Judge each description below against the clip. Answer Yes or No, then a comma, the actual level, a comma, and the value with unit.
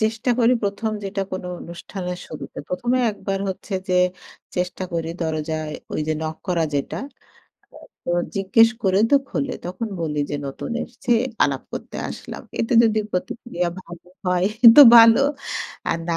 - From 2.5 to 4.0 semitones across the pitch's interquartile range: No, average, 4.9 semitones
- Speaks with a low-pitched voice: No, medium, 185 Hz